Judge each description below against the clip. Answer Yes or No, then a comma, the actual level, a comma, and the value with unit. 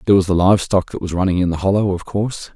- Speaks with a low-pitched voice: Yes, very low, 95 Hz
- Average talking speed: No, fast, 305 wpm